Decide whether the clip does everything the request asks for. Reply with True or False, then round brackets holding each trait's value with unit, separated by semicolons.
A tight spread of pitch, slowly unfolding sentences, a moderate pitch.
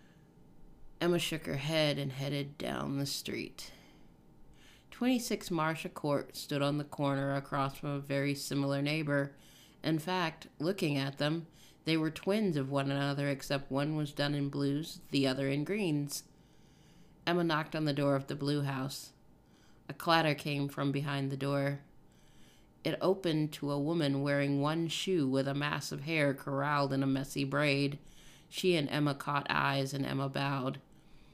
False (2.0 semitones; 165 wpm; 145 Hz)